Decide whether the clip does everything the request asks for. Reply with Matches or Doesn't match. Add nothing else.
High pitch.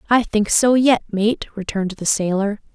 Matches